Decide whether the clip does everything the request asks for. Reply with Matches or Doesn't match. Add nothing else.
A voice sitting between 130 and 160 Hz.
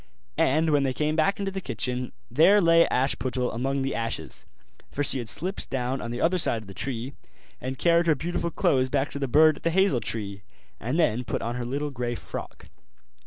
Matches